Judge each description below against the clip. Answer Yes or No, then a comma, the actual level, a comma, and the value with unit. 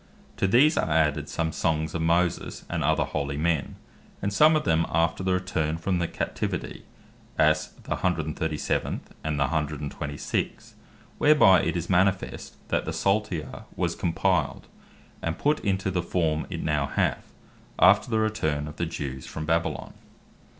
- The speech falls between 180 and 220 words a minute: No, average, 155 wpm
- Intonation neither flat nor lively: Yes, average, 3.5 semitones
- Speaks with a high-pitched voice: No, very low, 85 Hz